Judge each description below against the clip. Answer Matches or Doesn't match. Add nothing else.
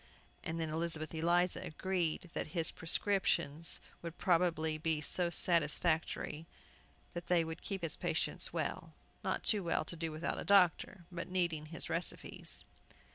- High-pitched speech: Doesn't match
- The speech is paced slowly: Doesn't match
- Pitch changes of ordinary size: Doesn't match